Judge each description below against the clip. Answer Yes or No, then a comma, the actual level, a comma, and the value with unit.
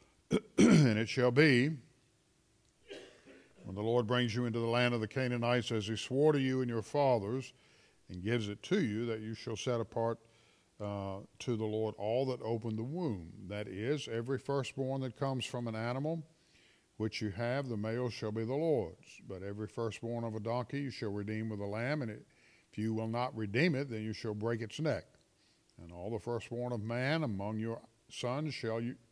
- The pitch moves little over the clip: No, average, 3.0 semitones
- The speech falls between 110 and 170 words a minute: No, average, 200 wpm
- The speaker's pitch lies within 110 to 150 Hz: Yes, low, 115 Hz